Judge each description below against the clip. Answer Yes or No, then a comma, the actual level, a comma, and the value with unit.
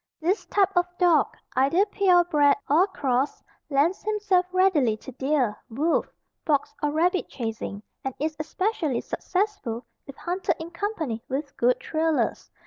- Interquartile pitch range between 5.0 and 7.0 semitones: Yes, wide, 5.4 semitones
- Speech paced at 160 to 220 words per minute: No, average, 140 wpm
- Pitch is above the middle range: Yes, very high, 315 Hz